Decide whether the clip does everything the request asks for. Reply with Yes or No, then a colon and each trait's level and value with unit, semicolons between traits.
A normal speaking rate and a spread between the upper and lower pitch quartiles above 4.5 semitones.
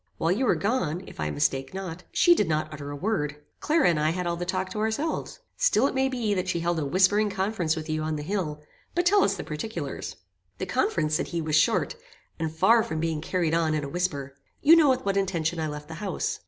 No: fast, 245 wpm; average, 5.0 semitones